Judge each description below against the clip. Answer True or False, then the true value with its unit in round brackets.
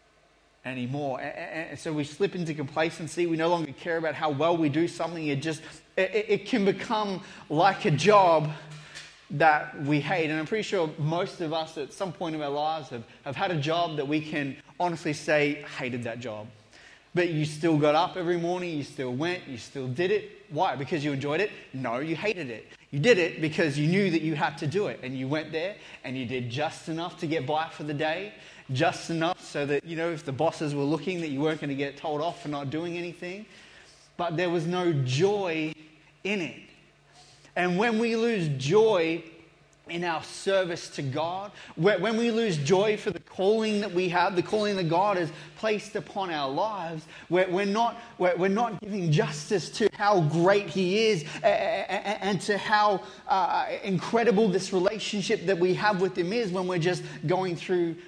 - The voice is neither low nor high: True (170 Hz)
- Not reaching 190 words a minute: False (200 wpm)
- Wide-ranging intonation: False (4.2 semitones)